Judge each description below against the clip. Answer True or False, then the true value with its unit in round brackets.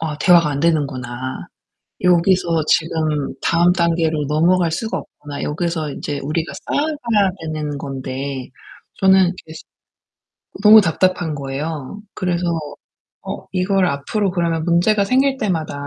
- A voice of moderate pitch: True (165 Hz)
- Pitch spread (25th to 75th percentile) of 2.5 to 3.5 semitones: False (3.9 semitones)